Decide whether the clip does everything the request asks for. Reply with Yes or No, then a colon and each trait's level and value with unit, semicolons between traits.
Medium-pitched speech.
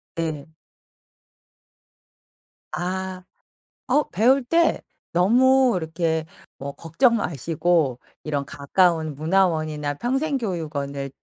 Yes: medium, 170 Hz